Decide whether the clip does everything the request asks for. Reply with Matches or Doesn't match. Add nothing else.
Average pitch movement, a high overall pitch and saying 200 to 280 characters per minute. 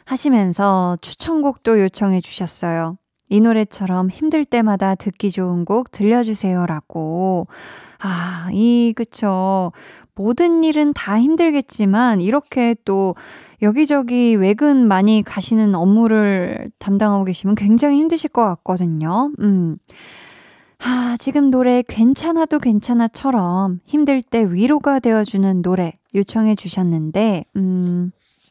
Matches